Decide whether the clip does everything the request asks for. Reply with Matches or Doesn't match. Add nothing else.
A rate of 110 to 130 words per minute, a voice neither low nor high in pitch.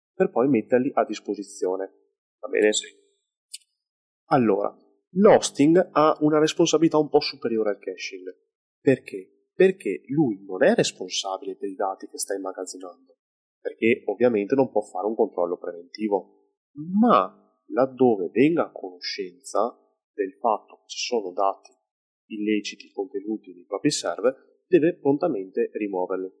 Matches